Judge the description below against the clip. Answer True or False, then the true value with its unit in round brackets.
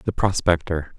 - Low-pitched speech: True (85 Hz)